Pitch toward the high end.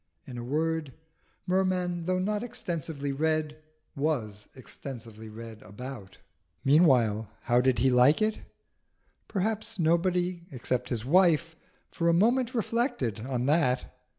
No: medium, 150 Hz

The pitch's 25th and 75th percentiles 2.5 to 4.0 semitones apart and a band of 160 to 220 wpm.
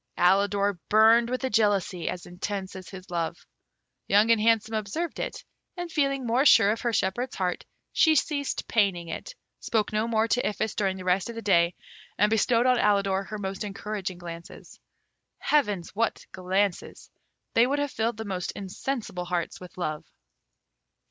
Yes: average, 3.7 semitones; average, 170 wpm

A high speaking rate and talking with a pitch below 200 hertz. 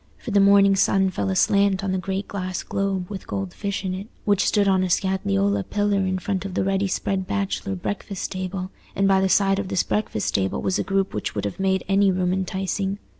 Yes: fast, 225 wpm; high, 190 Hz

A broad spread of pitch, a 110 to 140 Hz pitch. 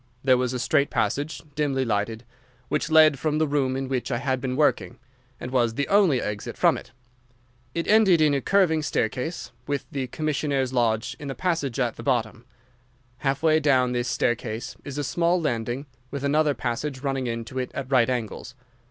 No: average, 3.5 semitones; low, 135 Hz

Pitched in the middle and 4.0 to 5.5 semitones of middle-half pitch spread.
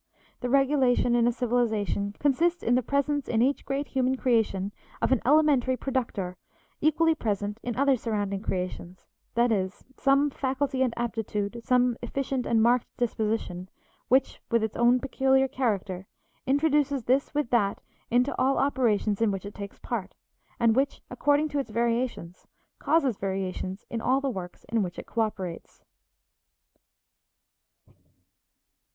No: high, 240 Hz; average, 4.5 semitones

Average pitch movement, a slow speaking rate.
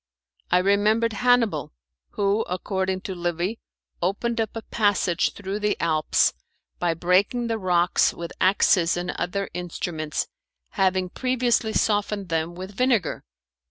Yes: average, 3.7 semitones; slow, 125 wpm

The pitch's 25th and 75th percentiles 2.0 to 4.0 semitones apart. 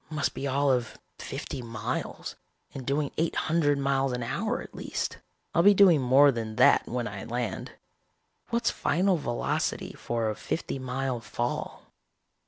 Yes: average, 3.5 semitones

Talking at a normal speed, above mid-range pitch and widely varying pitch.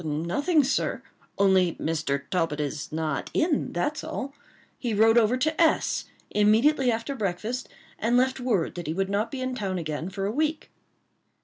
Yes: average, 170 wpm; high, 215 Hz; wide, 7.0 semitones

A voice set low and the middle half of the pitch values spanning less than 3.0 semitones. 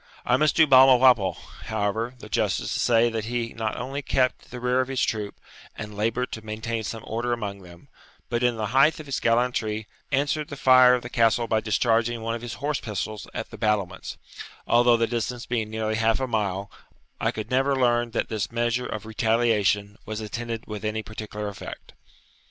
Yes: low, 115 Hz; narrow, 2.4 semitones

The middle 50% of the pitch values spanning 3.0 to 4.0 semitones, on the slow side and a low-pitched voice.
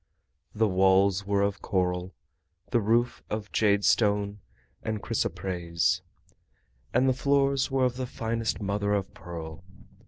Yes: average, 3.4 semitones; slow, 125 wpm; low, 100 Hz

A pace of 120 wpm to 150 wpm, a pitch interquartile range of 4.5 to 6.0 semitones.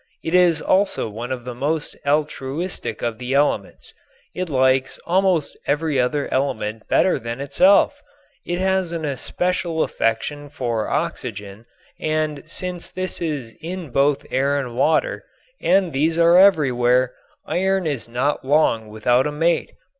Yes: average, 140 wpm; average, 5.1 semitones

